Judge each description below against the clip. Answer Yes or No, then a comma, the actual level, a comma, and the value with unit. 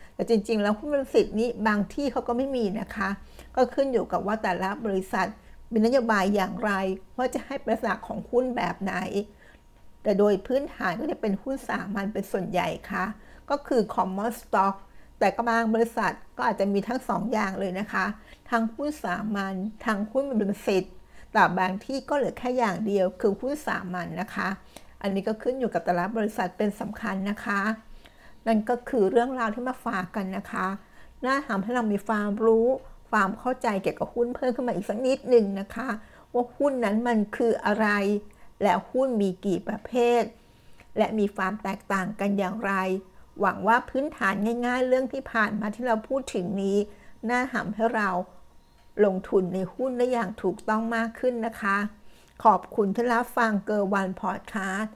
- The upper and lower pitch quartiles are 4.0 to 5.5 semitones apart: No, average, 3.4 semitones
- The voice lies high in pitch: Yes, high, 220 Hz